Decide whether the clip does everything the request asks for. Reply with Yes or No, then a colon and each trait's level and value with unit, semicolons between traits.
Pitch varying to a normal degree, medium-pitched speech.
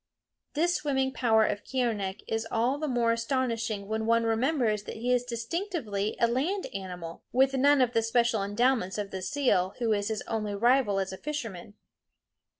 No: average, 4.1 semitones; high, 230 Hz